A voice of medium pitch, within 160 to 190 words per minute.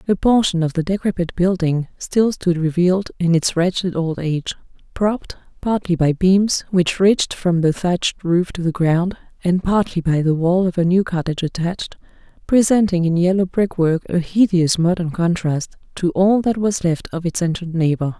Yes: medium, 175 Hz; average, 180 wpm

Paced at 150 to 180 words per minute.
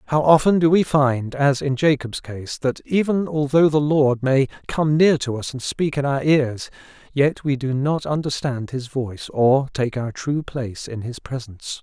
No: average, 200 wpm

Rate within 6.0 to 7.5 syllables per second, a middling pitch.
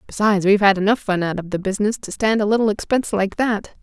No: 6.9 syllables/s; high, 205 Hz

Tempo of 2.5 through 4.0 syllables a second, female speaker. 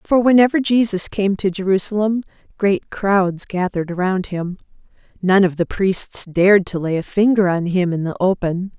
No: 4.9 syllables/s; female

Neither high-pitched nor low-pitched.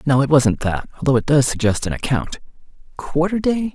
Yes: medium, 145 Hz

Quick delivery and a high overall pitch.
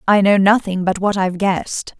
Yes: fast, 210 wpm; high, 195 Hz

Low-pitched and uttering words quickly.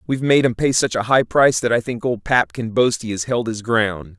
Yes: low, 120 Hz; fast, 285 wpm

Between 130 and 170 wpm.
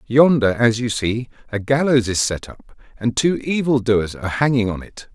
No: average, 200 wpm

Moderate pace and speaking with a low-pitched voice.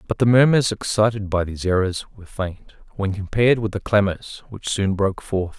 Yes: average, 195 wpm; low, 100 Hz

